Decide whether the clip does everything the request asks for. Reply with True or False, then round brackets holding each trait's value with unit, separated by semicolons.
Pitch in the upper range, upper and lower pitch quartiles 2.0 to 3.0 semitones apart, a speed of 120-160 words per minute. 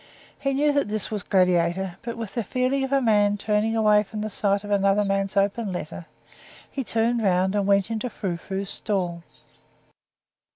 False (205 Hz; 2.6 semitones; 180 wpm)